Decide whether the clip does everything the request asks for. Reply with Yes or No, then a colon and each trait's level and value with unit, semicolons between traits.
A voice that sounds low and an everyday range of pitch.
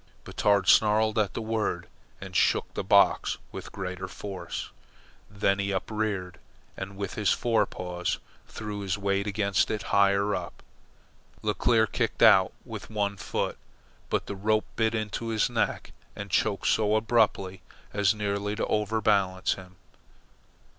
No: low, 100 Hz; narrow, 1.8 semitones